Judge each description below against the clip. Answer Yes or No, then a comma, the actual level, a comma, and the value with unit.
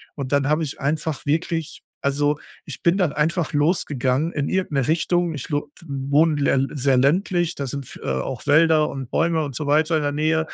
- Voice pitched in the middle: Yes, medium, 150 Hz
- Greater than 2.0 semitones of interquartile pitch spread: Yes, narrow, 2.6 semitones